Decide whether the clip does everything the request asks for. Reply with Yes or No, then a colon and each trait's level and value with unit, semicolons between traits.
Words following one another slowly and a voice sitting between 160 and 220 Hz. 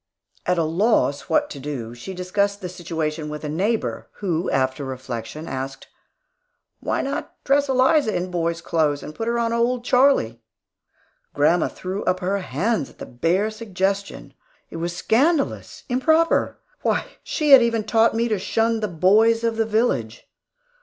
No: average, 160 wpm; high, 190 Hz